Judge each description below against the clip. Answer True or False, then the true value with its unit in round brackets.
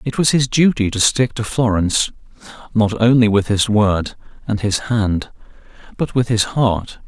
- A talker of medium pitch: False (110 Hz)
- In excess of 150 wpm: True (170 wpm)